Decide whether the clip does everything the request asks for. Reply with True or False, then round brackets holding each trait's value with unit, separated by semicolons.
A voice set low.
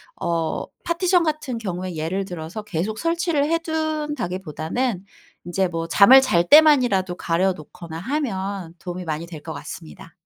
False (190 Hz)